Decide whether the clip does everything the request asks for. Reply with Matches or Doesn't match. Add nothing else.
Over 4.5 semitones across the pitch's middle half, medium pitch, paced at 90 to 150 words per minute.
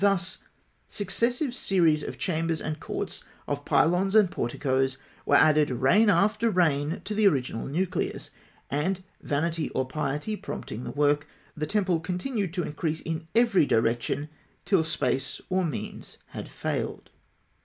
Matches